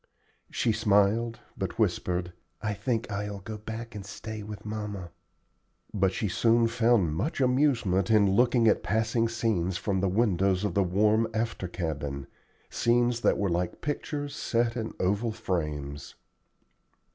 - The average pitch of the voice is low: Yes, low, 105 Hz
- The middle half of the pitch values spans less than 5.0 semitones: Yes, average, 3.5 semitones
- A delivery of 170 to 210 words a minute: No, average, 145 wpm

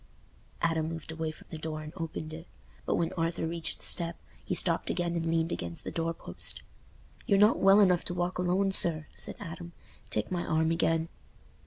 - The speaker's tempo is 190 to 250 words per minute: Yes, average, 195 wpm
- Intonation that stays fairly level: Yes, narrow, 1.5 semitones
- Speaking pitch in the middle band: Yes, medium, 165 Hz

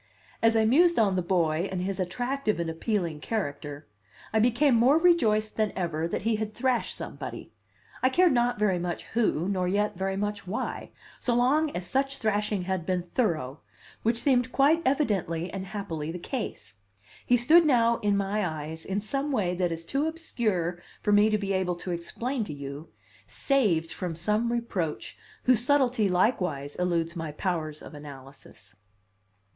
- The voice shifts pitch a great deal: Yes, wide, 5.8 semitones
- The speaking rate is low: No, average, 170 wpm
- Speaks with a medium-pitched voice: No, high, 200 Hz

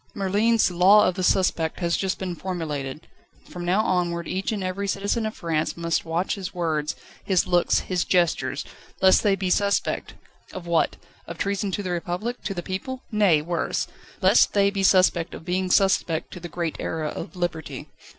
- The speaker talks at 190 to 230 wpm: No, average, 180 wpm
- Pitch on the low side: No, medium, 180 Hz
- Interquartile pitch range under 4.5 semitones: Yes, narrow, 2.5 semitones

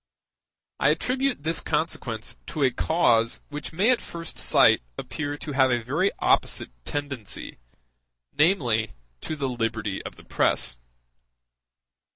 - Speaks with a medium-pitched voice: Yes, medium, 145 Hz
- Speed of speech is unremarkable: No, slow, 130 wpm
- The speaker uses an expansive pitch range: Yes, wide, 5.9 semitones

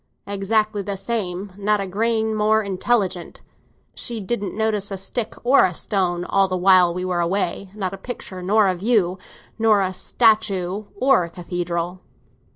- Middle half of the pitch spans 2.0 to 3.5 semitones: Yes, average, 2.9 semitones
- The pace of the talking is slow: No, average, 160 wpm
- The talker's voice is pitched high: Yes, high, 195 Hz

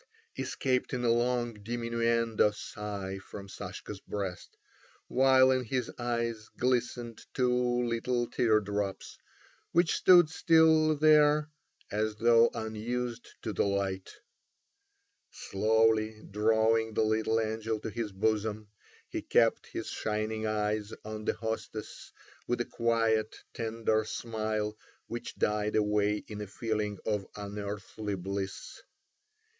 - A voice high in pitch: No, low, 110 Hz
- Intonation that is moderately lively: No, narrow, 2.2 semitones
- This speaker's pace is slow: Yes, slow, 120 wpm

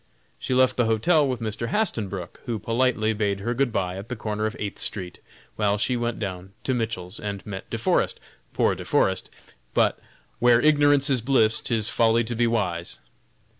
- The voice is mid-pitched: No, low, 110 Hz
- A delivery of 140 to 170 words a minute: No, average, 185 wpm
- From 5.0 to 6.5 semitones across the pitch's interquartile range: No, average, 3.2 semitones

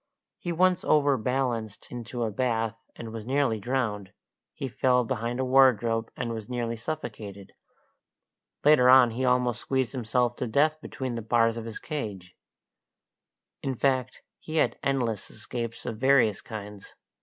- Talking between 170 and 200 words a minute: No, average, 145 wpm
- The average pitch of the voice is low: Yes, low, 120 Hz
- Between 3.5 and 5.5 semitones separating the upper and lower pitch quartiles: No, average, 2.8 semitones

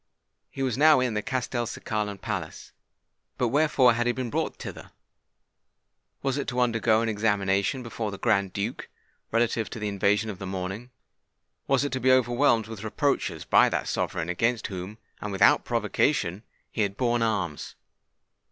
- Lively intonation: No, average, 3.6 semitones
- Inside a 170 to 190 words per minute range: No, average, 160 wpm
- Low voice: Yes, low, 115 Hz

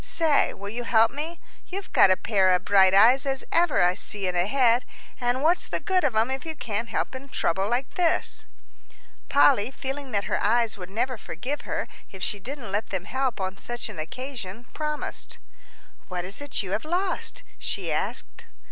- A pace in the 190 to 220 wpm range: Yes, average, 195 wpm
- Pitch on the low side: No, high, 240 Hz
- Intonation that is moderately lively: No, wide, 5.8 semitones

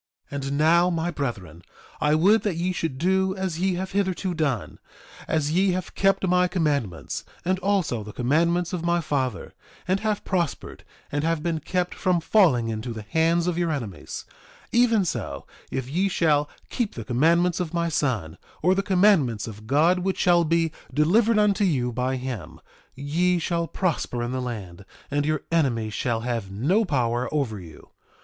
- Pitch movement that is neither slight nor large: No, wide, 6.2 semitones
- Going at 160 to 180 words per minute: Yes, average, 175 wpm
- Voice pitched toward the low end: No, medium, 160 Hz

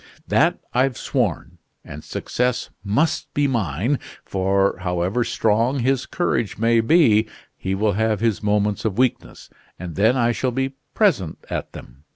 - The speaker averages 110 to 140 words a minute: No, average, 150 wpm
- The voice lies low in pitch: Yes, low, 110 Hz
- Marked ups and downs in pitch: No, average, 4.5 semitones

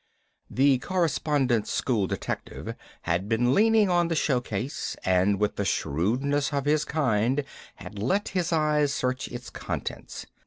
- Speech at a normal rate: Yes, average, 145 wpm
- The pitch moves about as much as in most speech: No, wide, 6.1 semitones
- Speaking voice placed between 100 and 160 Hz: Yes, low, 135 Hz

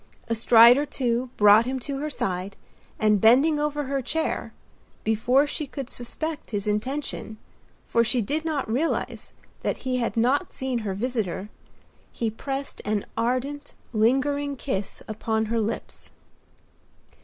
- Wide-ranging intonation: No, average, 4.3 semitones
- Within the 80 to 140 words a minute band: Yes, slow, 135 wpm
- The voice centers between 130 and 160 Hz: No, high, 245 Hz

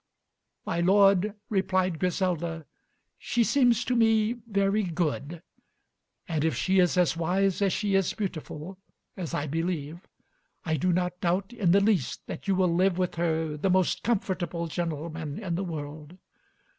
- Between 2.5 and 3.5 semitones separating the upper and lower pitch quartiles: Yes, average, 3.0 semitones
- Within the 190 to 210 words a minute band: No, average, 155 wpm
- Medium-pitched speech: Yes, medium, 180 Hz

